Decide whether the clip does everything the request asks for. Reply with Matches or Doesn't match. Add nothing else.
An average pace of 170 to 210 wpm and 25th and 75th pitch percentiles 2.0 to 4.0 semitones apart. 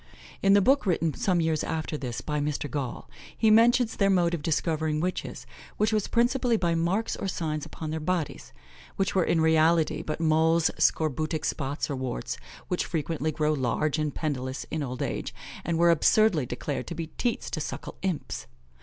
Matches